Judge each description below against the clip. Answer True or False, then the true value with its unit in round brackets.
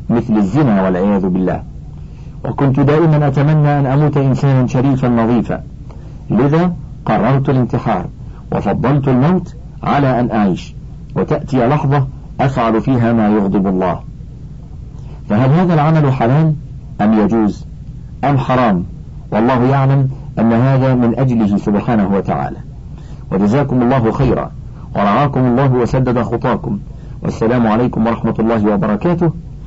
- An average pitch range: True (3.9 semitones)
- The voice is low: True (130 Hz)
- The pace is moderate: True (110 wpm)